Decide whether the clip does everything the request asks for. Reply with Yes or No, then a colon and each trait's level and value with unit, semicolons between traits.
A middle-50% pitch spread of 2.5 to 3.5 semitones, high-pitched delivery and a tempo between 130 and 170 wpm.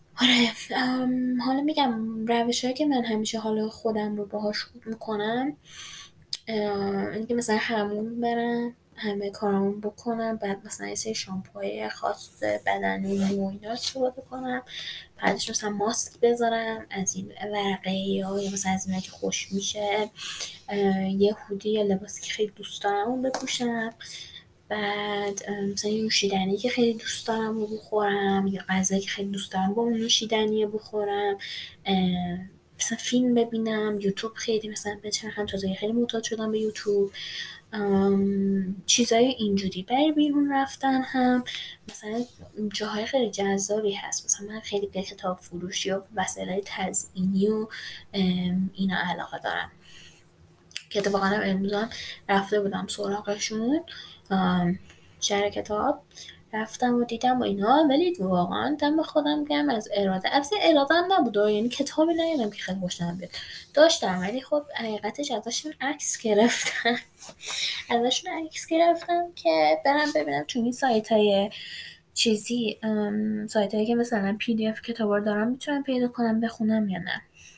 Yes: average, 3.1 semitones; high, 215 Hz; average, 140 wpm